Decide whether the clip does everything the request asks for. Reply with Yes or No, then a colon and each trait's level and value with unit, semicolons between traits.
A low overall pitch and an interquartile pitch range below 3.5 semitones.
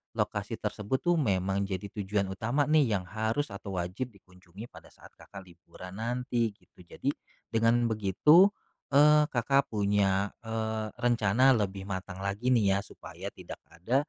No: low, 110 Hz; average, 4.3 semitones